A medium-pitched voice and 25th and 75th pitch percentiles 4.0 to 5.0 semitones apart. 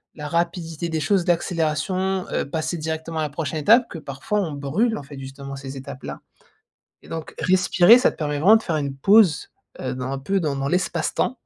Yes: medium, 160 Hz; average, 4.4 semitones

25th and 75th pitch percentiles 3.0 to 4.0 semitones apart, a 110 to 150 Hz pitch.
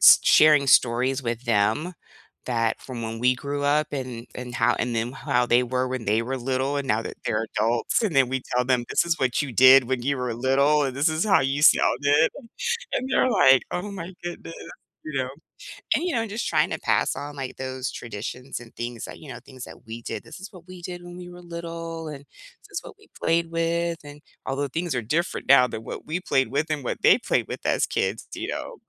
No: average, 5.1 semitones; low, 135 Hz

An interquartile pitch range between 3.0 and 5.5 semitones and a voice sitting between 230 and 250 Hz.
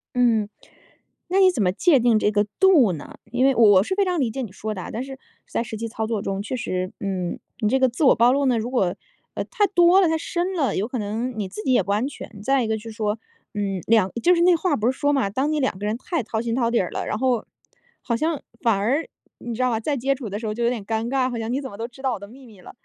Yes: average, 4.2 semitones; high, 235 Hz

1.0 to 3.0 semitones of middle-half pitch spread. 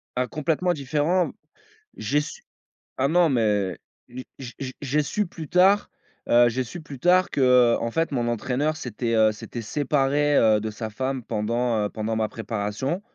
No: average, 5.0 semitones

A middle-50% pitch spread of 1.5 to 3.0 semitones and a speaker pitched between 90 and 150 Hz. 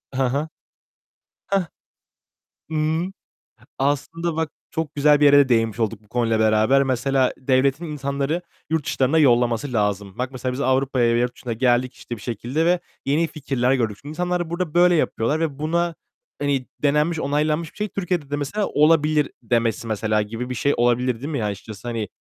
No: average, 4.4 semitones; low, 135 Hz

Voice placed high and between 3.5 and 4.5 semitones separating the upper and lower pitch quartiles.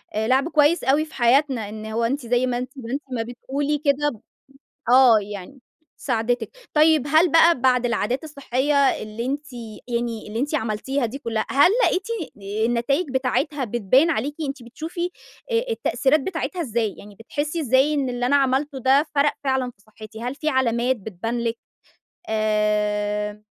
Yes: very high, 255 Hz; average, 4.1 semitones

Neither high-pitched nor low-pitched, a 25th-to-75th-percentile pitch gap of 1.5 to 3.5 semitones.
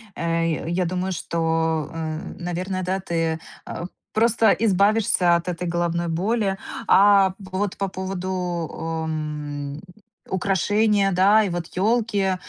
Yes: medium, 180 Hz; average, 2.9 semitones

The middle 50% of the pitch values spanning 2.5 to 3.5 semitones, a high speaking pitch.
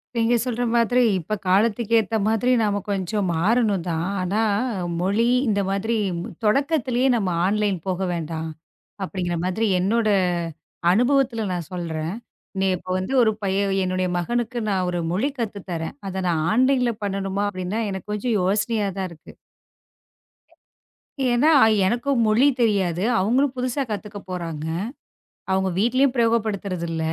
No: average, 4.1 semitones; high, 205 Hz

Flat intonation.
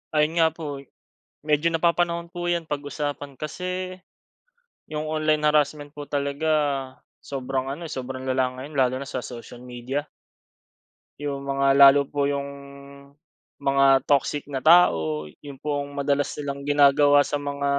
Yes: narrow, 1.9 semitones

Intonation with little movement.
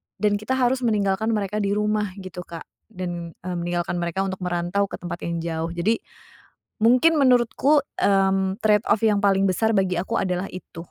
No: average, 3.2 semitones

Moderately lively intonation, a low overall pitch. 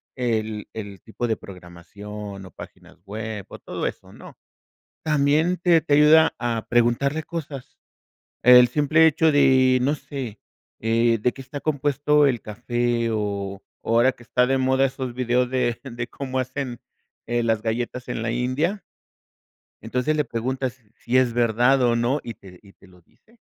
Yes: average, 3.5 semitones; low, 125 Hz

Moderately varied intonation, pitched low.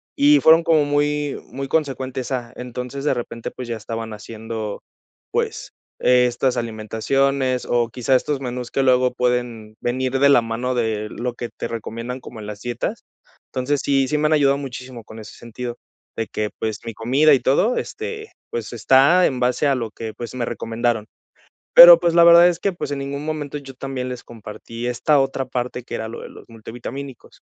Yes: average, 3.2 semitones; low, 125 Hz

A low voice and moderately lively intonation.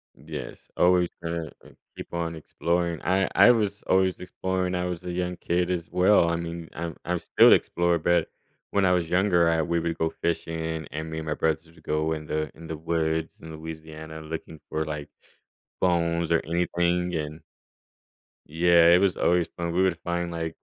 No: very low, 85 Hz; narrow, 1.7 semitones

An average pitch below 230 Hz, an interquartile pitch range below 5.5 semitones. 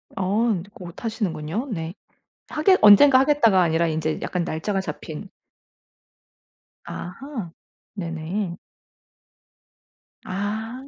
Yes: high, 195 Hz; average, 5.1 semitones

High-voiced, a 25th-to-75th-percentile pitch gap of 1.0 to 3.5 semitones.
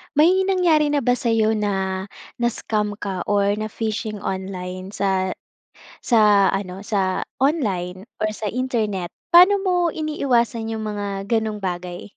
No: high, 210 Hz; average, 4.0 semitones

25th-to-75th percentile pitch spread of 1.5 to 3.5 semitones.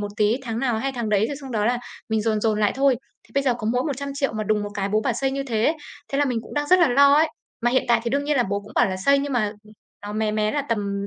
No: average, 4.5 semitones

